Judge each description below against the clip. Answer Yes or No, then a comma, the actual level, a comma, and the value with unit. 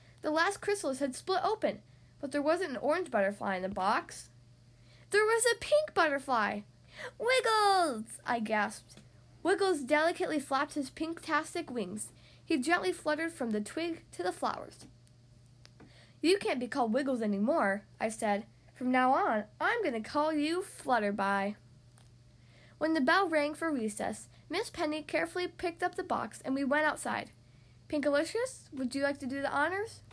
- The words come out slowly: No, average, 160 wpm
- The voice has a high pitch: Yes, very high, 285 Hz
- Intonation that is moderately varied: No, wide, 8.4 semitones